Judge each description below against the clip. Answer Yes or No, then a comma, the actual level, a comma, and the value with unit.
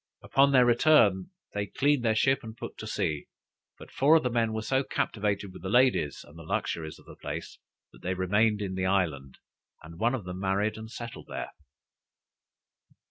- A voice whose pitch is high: No, low, 105 Hz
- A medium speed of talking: Yes, average, 190 wpm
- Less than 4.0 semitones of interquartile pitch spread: No, average, 4.6 semitones